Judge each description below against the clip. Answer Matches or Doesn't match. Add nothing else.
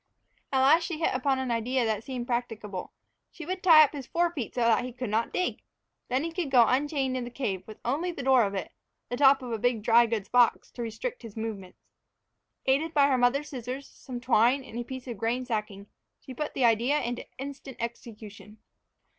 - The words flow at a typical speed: Doesn't match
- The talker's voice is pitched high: Matches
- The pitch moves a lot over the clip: Doesn't match